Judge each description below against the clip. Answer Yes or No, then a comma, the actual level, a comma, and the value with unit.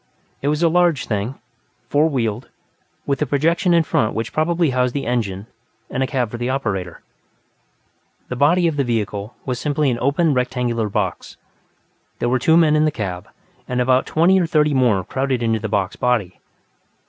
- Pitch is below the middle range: Yes, low, 130 Hz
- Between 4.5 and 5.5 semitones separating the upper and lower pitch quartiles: Yes, average, 5.0 semitones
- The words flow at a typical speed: Yes, average, 185 wpm